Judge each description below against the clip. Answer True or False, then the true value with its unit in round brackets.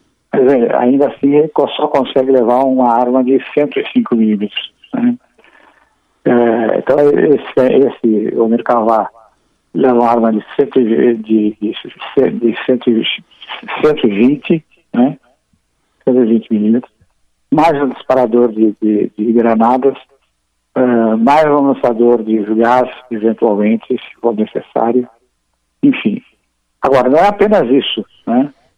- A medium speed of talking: False (115 wpm)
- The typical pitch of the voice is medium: False (120 Hz)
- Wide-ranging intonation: False (3.5 semitones)